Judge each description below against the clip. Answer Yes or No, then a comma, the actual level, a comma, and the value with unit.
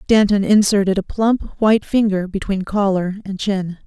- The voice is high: Yes, high, 200 Hz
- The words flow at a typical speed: Yes, average, 155 wpm